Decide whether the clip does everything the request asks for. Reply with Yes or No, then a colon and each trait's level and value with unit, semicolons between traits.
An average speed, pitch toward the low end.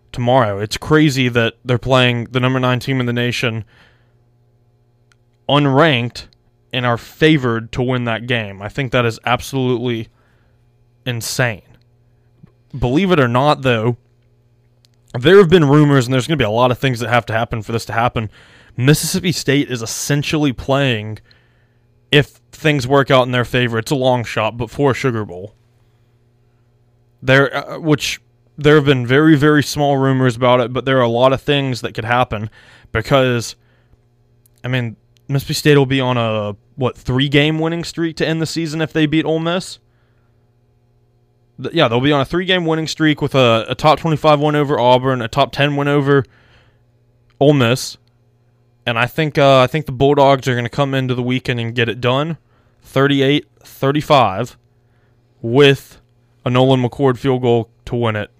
Yes: average, 175 wpm; low, 125 Hz